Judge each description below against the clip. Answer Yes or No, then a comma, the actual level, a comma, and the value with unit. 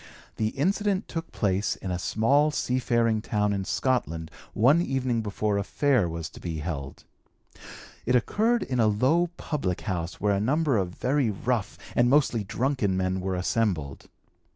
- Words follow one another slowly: No, average, 160 wpm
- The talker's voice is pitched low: Yes, low, 110 Hz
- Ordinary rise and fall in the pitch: No, wide, 6.1 semitones